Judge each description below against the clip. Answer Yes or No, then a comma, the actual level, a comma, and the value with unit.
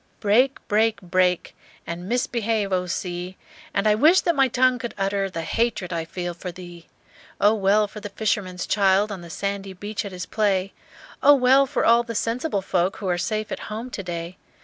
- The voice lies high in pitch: Yes, high, 200 Hz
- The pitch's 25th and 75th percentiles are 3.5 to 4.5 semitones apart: Yes, average, 3.8 semitones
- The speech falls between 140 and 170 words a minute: No, average, 195 wpm